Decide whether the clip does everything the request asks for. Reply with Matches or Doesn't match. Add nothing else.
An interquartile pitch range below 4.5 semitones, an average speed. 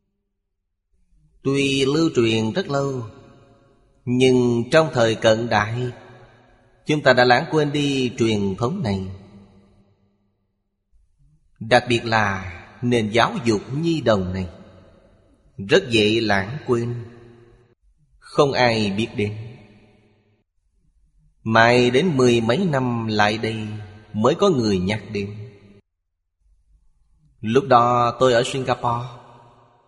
Doesn't match